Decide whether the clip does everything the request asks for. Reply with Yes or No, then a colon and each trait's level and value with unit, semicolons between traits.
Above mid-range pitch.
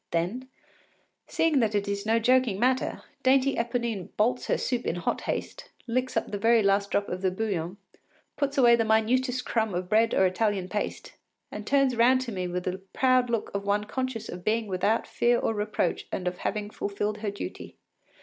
Yes: high, 220 Hz